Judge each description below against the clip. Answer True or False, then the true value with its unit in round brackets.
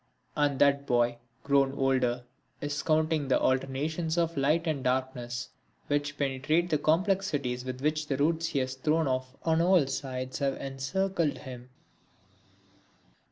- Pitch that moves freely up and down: False (3.3 semitones)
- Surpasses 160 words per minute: False (140 wpm)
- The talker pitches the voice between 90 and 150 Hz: True (140 Hz)